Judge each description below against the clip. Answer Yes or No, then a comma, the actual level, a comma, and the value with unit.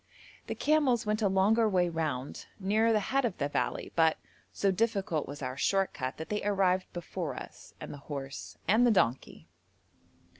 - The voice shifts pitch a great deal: Yes, wide, 5.8 semitones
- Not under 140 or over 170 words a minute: No, average, 180 wpm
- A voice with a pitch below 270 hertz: Yes, high, 190 Hz